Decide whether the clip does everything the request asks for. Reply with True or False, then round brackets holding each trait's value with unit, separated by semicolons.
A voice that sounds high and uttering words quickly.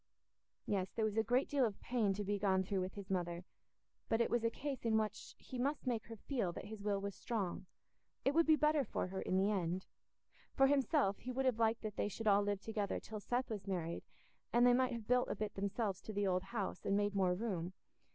True (210 Hz; 240 wpm)